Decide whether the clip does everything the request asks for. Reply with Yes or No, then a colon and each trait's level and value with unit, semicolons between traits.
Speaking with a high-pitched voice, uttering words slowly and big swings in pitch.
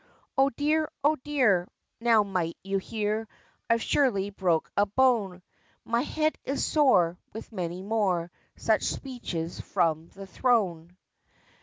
Yes: high, 205 Hz; slow, 130 wpm; wide, 6.0 semitones